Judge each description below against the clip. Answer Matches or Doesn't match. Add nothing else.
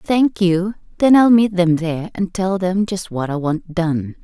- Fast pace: Matches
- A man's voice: Doesn't match